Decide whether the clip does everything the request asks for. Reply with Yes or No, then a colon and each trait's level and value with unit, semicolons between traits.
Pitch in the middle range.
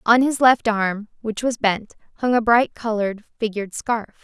No: high, 225 Hz